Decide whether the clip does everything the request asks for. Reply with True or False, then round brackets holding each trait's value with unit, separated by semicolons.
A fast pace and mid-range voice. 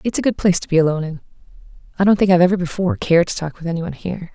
True (275 wpm; 175 Hz)